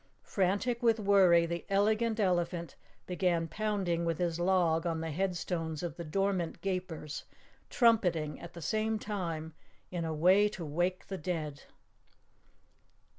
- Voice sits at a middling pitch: Yes, medium, 180 Hz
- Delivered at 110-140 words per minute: Yes, slow, 135 wpm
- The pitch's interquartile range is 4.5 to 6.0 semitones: No, average, 3.2 semitones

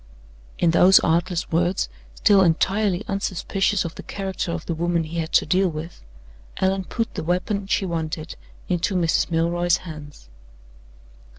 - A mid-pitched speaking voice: Yes, medium, 175 Hz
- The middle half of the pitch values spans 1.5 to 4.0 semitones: Yes, narrow, 2.6 semitones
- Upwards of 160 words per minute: No, average, 150 wpm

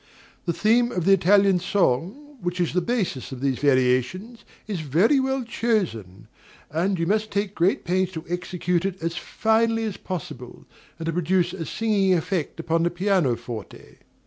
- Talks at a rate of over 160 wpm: Yes, average, 170 wpm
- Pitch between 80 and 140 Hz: No, medium, 180 Hz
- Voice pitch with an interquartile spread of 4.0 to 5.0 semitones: Yes, average, 4.3 semitones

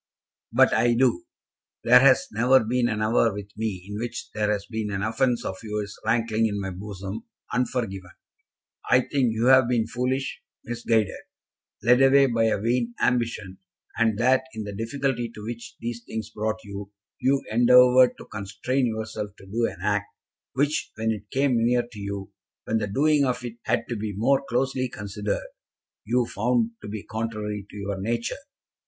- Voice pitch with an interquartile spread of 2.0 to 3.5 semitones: Yes, average, 3.0 semitones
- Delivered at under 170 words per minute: No, average, 175 wpm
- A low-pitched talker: Yes, low, 115 Hz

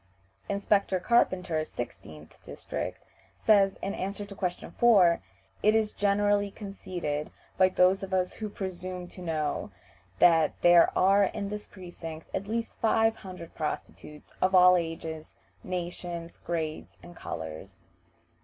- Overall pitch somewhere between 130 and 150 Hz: No, medium, 185 Hz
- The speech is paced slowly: Yes, slow, 130 wpm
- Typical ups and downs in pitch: Yes, average, 3.1 semitones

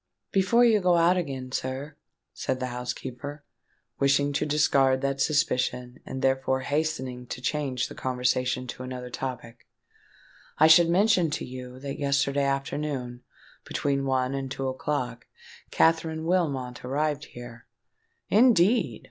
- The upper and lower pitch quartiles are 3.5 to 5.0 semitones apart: No, average, 3.1 semitones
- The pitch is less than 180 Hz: Yes, low, 135 Hz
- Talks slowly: Yes, slow, 125 wpm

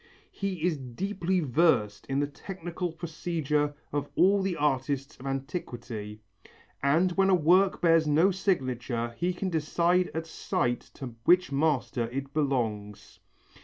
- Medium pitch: Yes, medium, 150 Hz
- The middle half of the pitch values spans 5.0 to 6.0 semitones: Yes, average, 5.3 semitones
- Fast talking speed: No, slow, 135 wpm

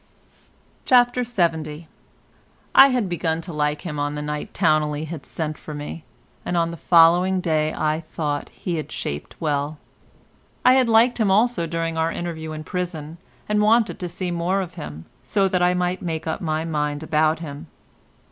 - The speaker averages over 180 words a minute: No, average, 175 wpm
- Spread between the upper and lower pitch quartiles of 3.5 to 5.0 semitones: No, average, 2.9 semitones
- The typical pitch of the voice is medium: Yes, medium, 165 Hz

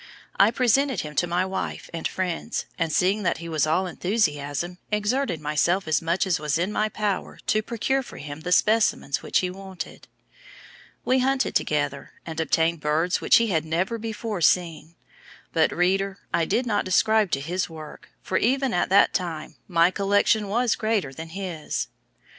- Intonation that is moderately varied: Yes, average, 4.7 semitones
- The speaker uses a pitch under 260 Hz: Yes, medium, 185 Hz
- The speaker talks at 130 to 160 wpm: No, average, 175 wpm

